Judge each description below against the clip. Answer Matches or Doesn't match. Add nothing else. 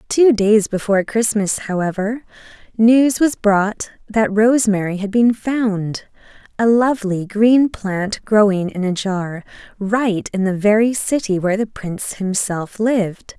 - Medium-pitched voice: Doesn't match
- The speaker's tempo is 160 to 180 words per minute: Doesn't match